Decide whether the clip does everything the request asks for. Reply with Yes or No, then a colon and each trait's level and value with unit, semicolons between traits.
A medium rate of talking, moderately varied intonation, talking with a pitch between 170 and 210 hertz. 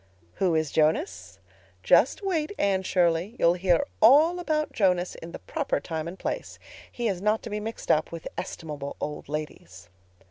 No: average, 170 wpm; wide, 6.2 semitones; medium, 185 Hz